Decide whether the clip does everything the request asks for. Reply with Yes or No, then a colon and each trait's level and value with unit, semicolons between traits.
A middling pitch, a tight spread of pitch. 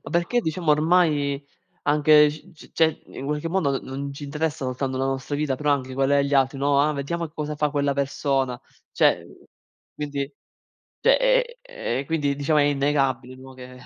Yes: medium, 145 Hz; narrow, 1.9 semitones